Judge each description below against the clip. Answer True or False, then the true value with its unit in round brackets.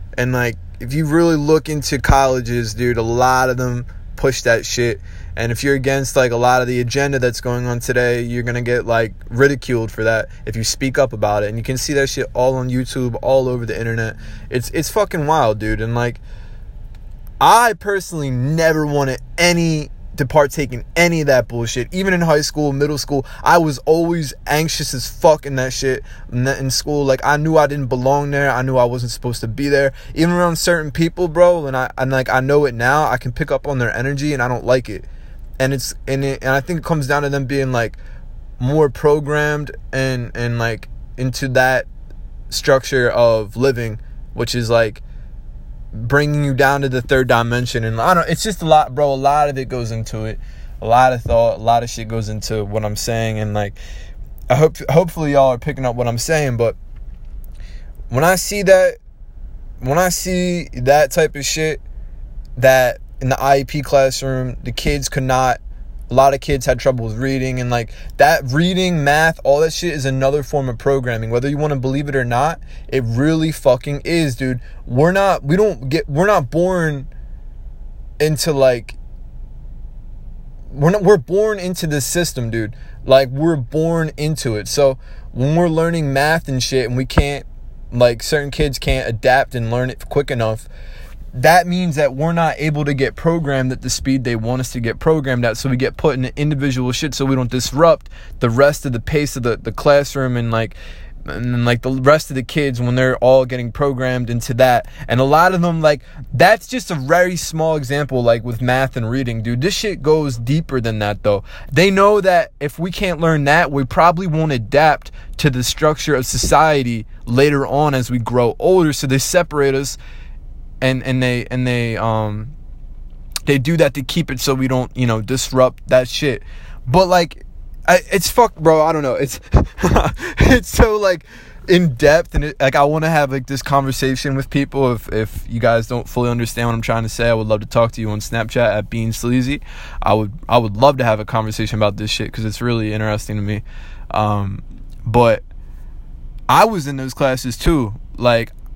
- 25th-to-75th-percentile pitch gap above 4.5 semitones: False (4.0 semitones)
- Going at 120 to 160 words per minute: False (205 wpm)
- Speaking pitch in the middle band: False (130 Hz)